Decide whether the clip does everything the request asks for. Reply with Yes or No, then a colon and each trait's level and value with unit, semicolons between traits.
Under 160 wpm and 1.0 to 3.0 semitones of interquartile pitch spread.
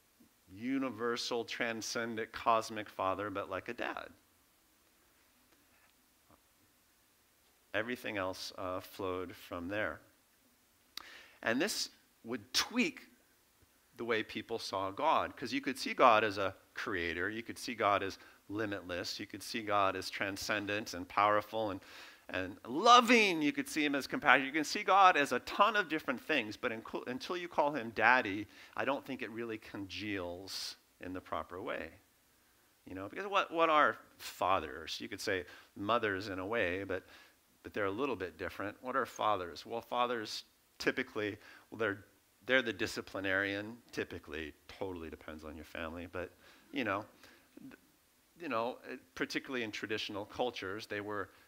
No: average, 150 wpm; average, 4.8 semitones